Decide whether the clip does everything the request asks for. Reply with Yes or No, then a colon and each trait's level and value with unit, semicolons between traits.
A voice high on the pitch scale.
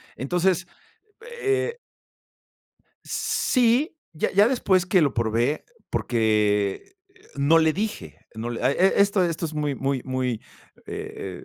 No: medium, 155 Hz